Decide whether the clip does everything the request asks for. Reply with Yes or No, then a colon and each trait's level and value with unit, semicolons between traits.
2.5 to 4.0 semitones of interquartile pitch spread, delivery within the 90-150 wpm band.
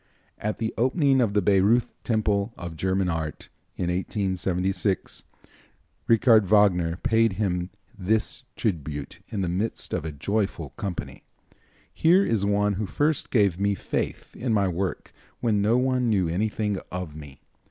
Yes: average, 3.6 semitones; average, 145 wpm